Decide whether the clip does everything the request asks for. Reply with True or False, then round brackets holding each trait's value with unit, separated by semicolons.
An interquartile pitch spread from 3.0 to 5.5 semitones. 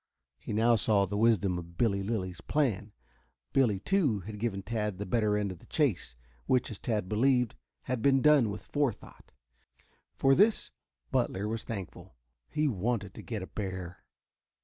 True (4.1 semitones)